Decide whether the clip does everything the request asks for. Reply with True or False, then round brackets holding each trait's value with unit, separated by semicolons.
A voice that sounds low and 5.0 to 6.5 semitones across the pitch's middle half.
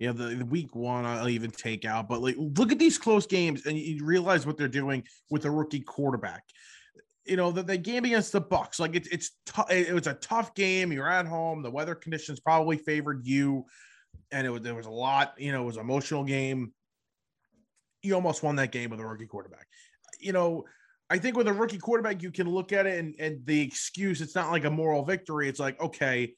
False (155 Hz; 5.5 semitones)